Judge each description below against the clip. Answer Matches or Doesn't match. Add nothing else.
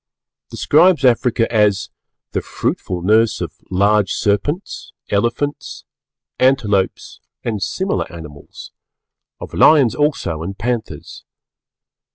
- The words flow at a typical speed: Doesn't match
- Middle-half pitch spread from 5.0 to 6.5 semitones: Matches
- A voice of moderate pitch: Doesn't match